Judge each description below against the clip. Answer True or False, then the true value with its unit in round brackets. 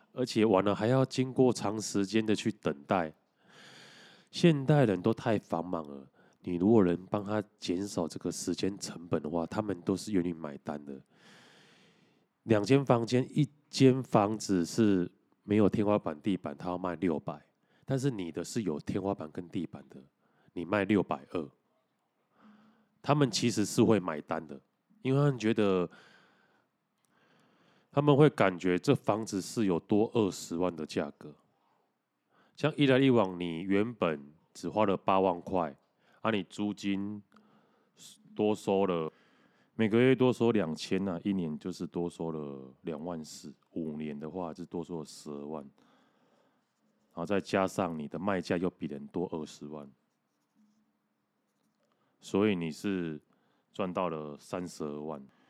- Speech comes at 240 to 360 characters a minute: False (210 characters per minute)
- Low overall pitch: True (100 Hz)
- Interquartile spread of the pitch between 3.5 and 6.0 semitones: True (5.2 semitones)